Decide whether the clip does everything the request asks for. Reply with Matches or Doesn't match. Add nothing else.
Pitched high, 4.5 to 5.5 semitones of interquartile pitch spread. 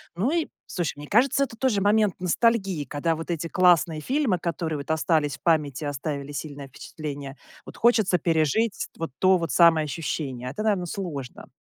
Doesn't match